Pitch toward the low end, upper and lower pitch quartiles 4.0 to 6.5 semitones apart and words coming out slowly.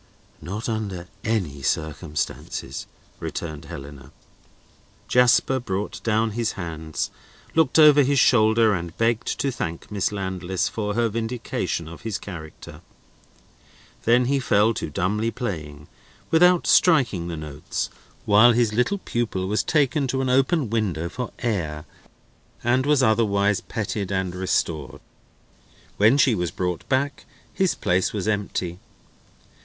Yes: low, 105 Hz; wide, 5.6 semitones; slow, 130 wpm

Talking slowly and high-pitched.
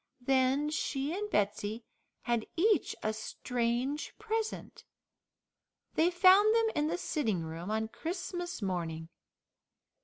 Yes: slow, 115 wpm; very high, 270 Hz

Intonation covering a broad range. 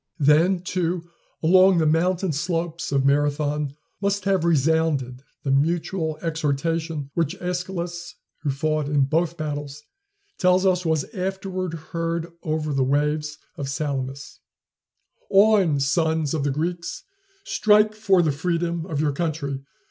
No: average, 3.3 semitones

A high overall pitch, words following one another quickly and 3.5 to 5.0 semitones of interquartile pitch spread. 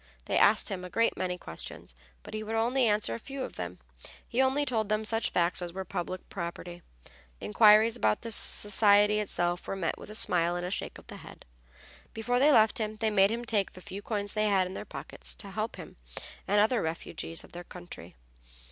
Yes: high, 205 Hz; fast, 215 wpm; average, 3.8 semitones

